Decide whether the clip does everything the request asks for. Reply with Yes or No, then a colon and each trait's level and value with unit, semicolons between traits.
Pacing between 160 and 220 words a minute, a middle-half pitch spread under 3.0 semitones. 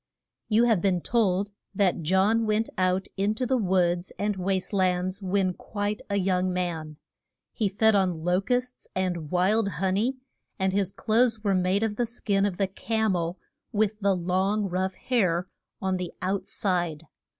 Yes: average, 170 wpm; narrow, 2.6 semitones